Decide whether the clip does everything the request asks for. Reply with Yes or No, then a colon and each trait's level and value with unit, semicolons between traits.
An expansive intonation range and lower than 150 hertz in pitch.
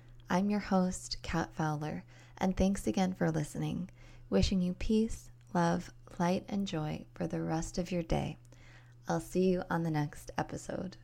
No: wide, 6.7 semitones; medium, 165 Hz